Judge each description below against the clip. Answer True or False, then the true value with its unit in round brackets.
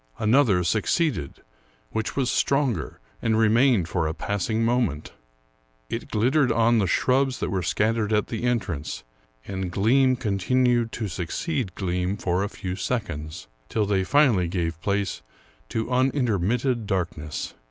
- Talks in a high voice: False (110 Hz)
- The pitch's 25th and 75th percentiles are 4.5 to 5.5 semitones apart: True (5.2 semitones)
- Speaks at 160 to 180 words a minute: False (135 wpm)